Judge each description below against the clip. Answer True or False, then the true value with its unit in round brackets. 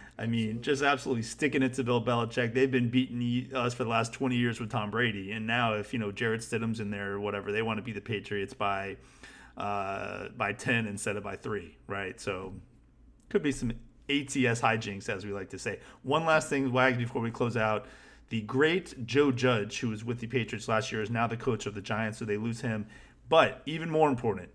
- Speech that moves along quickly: True (225 wpm)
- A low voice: True (115 Hz)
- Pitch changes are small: False (3.1 semitones)